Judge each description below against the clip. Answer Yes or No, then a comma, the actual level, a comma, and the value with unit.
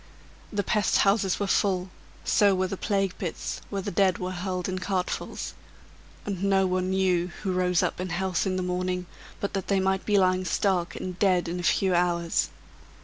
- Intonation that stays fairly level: Yes, narrow, 1.3 semitones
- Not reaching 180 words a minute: No, average, 195 wpm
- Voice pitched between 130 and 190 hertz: Yes, medium, 185 Hz